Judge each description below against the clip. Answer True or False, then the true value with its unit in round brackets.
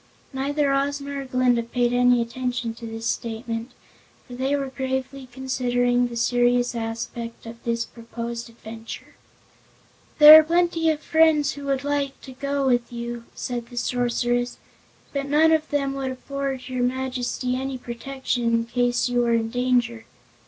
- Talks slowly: False (155 wpm)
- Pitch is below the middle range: False (250 Hz)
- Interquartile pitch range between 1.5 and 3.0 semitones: True (2.5 semitones)